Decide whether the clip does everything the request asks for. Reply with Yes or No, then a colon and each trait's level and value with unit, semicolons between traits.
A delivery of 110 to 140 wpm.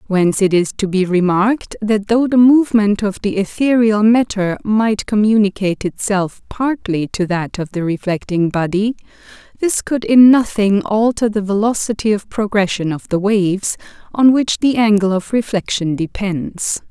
No: average, 155 wpm